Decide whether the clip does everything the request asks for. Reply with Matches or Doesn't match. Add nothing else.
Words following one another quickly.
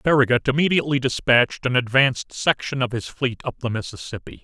Doesn't match